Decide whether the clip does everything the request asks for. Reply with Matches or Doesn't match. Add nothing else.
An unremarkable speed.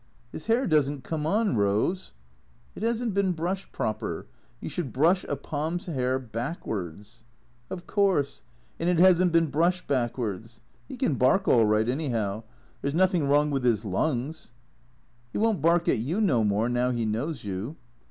Matches